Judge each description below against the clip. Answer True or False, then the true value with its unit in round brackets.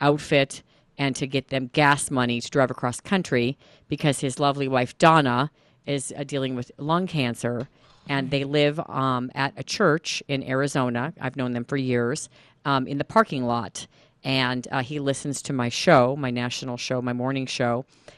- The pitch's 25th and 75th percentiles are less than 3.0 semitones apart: True (2.6 semitones)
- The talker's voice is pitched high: False (135 Hz)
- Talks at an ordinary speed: True (180 wpm)